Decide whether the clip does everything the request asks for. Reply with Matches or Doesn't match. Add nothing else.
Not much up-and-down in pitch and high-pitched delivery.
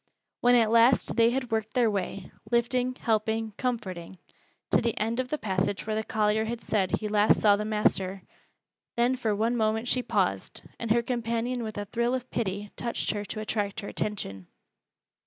Matches